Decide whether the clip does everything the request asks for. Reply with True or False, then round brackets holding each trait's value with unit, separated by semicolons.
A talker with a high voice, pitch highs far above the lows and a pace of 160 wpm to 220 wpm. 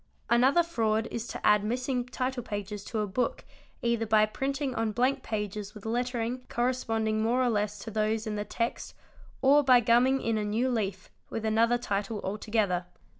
False (225 Hz; 2.8 semitones; 175 wpm)